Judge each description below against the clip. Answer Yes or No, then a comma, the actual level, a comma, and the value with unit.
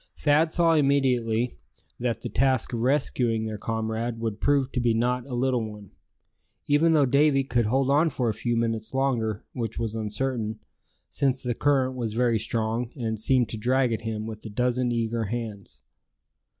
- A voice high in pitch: No, low, 120 Hz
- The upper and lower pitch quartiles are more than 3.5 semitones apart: No, average, 3.0 semitones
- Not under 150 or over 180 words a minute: Yes, average, 175 wpm